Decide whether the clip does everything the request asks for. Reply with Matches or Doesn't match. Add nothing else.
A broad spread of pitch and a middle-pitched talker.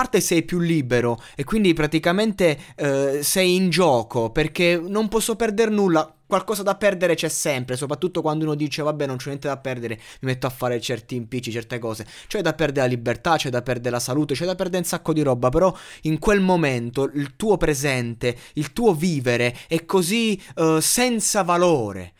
Matches